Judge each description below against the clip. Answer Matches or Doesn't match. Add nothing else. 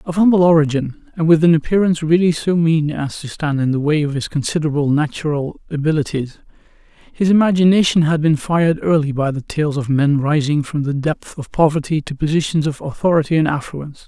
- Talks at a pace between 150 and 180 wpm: Doesn't match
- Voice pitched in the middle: Matches